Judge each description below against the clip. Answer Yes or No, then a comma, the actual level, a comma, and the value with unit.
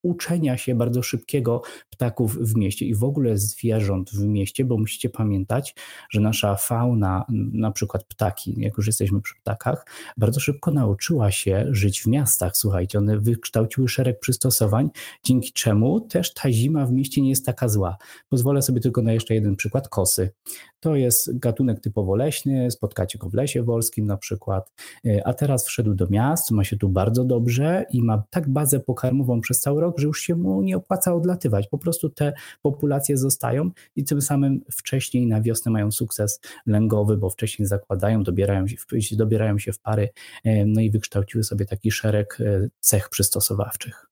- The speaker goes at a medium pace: No, fast, 170 wpm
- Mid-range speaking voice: No, low, 115 Hz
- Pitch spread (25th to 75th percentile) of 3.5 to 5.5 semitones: Yes, average, 4.2 semitones